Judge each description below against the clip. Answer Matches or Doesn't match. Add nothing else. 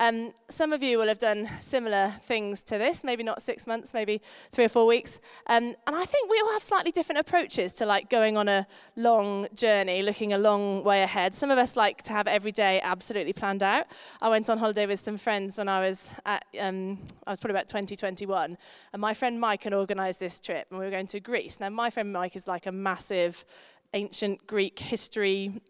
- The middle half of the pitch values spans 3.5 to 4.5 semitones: Doesn't match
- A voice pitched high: Matches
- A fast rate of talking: Matches